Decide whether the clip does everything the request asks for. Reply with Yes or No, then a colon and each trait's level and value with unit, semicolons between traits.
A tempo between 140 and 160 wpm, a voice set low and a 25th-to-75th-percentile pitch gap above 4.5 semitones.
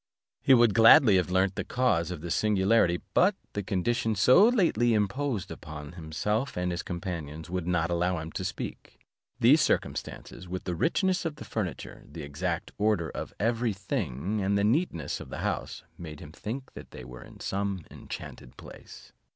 No: average, 175 wpm; very low, 95 Hz; average, 5.1 semitones